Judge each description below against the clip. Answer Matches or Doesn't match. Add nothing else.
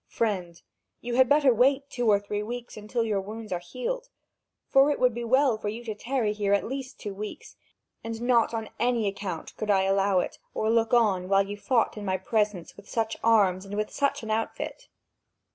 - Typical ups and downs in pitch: Matches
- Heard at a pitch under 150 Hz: Doesn't match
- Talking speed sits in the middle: Doesn't match